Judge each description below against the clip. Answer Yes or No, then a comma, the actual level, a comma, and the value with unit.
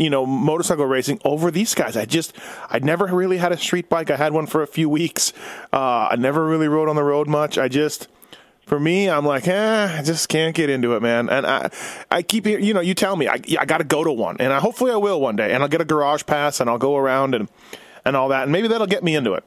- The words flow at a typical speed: No, fast, 275 wpm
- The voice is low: No, medium, 155 Hz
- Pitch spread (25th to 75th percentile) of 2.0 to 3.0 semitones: No, average, 3.8 semitones